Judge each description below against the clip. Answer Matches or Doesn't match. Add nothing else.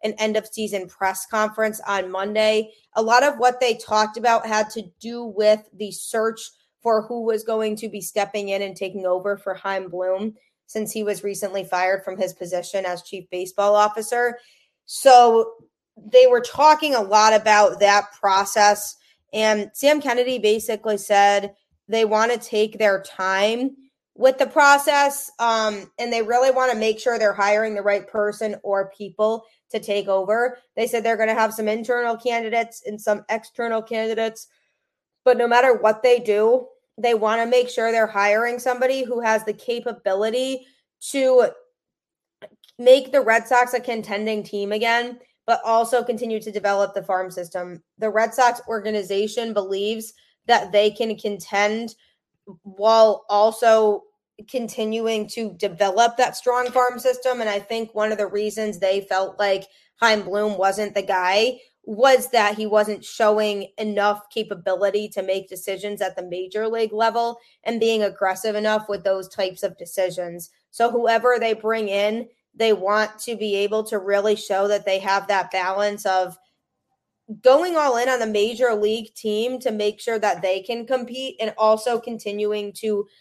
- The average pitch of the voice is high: Matches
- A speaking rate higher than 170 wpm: Doesn't match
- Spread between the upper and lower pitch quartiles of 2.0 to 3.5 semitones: Matches